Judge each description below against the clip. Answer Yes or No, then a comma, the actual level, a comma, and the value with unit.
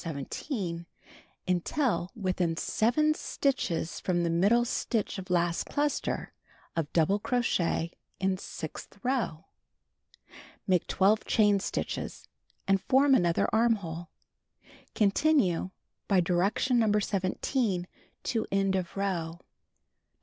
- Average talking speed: No, slow, 105 wpm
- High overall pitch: Yes, high, 195 Hz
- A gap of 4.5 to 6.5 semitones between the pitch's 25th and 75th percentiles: Yes, average, 4.8 semitones